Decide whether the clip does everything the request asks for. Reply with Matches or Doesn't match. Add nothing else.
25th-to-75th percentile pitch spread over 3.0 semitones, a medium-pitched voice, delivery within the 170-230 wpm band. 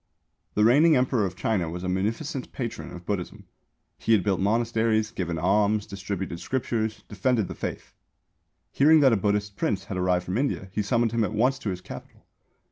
Doesn't match